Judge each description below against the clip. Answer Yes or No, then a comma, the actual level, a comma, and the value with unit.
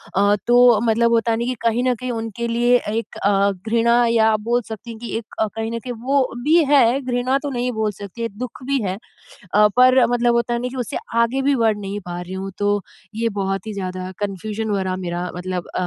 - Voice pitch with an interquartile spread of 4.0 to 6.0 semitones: No, average, 3.1 semitones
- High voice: Yes, high, 230 Hz